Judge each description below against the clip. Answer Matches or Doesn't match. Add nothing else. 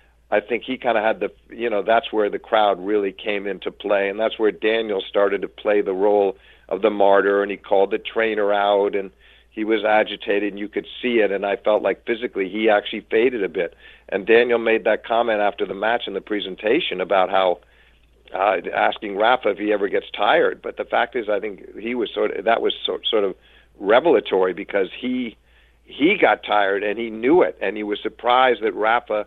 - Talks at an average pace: Doesn't match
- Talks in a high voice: Doesn't match